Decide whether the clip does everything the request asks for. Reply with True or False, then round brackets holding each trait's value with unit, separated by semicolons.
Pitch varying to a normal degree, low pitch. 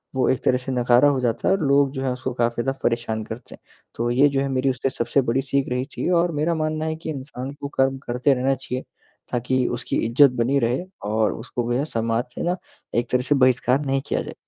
False (2.2 semitones; 130 Hz)